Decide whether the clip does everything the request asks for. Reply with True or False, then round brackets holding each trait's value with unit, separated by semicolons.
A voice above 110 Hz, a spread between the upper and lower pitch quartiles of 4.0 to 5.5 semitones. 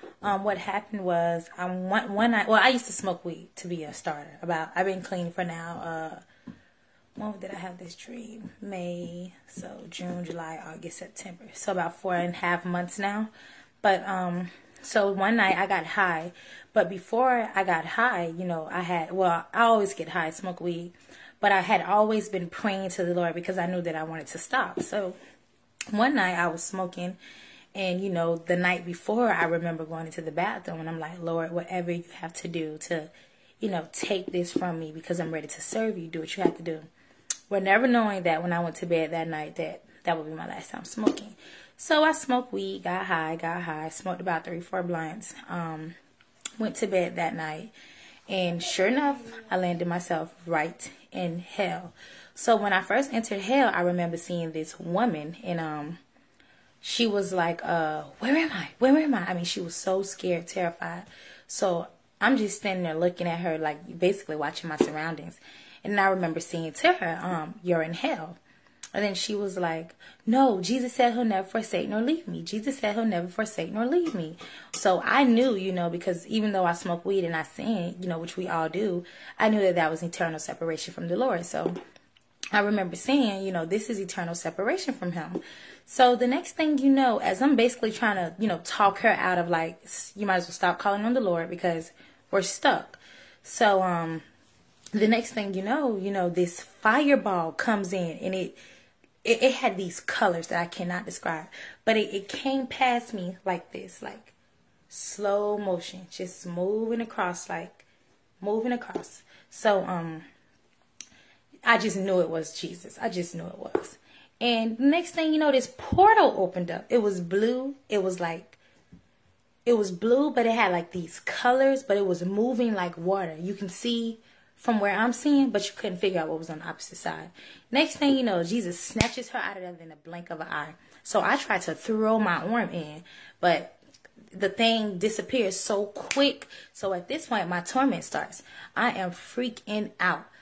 True (185 Hz; 4.5 semitones)